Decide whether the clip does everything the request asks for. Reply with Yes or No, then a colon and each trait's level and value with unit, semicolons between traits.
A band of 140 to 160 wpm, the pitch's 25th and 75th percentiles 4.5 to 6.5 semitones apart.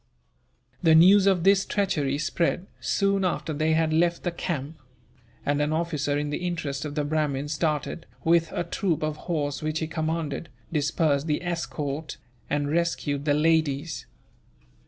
No: average, 155 wpm; narrow, 2.5 semitones